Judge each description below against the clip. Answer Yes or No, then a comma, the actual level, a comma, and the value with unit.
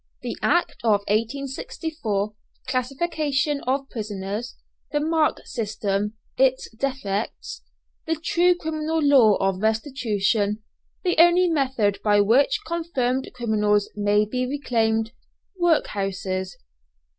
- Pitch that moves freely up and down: Yes, wide, 5.9 semitones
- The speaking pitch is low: No, high, 245 Hz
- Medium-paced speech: No, slow, 100 wpm